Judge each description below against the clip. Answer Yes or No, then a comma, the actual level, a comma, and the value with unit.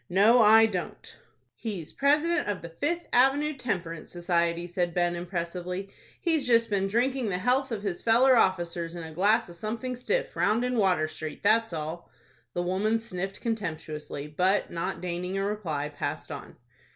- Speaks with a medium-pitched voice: No, high, 195 Hz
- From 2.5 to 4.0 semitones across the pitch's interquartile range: No, average, 5.1 semitones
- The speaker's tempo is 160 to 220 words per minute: Yes, average, 165 wpm